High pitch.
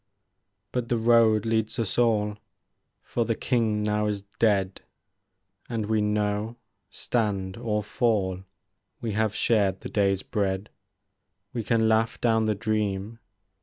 No: low, 110 Hz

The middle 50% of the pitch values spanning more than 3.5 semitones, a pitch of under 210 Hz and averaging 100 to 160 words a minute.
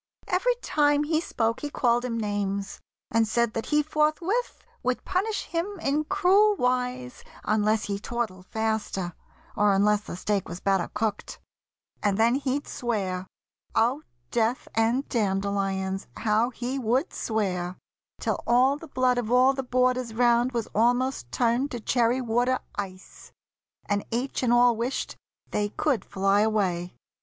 No: average, 4.0 semitones; high, 235 Hz; average, 150 wpm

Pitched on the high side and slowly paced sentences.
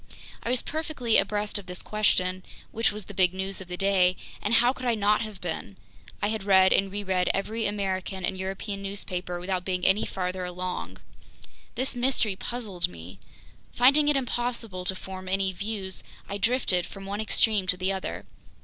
No: high, 195 Hz; average, 180 wpm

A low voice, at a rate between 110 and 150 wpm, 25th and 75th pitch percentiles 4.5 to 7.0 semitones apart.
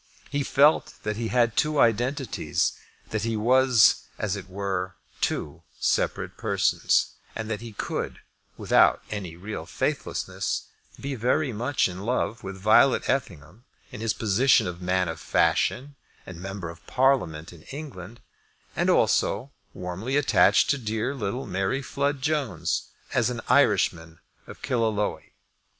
Yes: low, 110 Hz; average, 140 wpm; wide, 5.6 semitones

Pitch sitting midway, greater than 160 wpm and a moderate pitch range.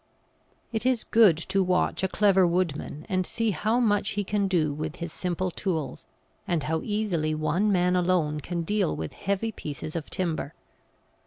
Yes: medium, 180 Hz; average, 170 wpm; average, 4.2 semitones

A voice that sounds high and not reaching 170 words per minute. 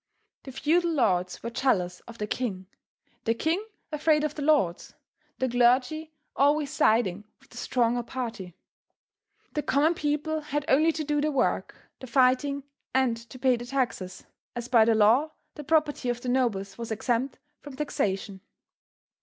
Yes: very high, 255 Hz; average, 160 wpm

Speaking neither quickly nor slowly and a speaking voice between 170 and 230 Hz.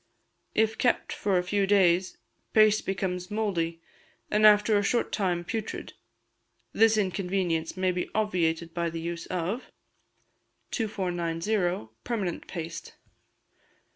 No: slow, 115 wpm; medium, 185 Hz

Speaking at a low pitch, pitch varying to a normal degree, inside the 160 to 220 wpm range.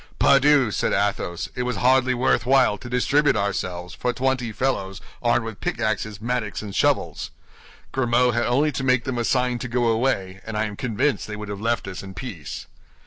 Yes: low, 120 Hz; average, 3.5 semitones; average, 195 wpm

